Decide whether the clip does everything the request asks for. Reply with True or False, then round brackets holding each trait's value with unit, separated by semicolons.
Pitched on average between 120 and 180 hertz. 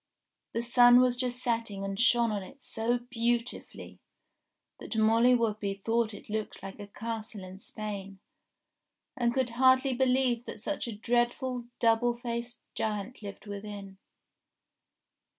False (230 Hz)